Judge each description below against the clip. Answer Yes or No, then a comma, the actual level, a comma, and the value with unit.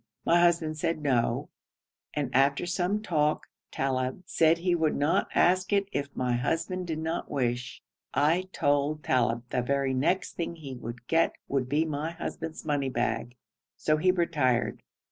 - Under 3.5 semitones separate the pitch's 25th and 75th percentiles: No, average, 4.5 semitones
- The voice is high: No, medium, 150 Hz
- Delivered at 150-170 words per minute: Yes, average, 165 wpm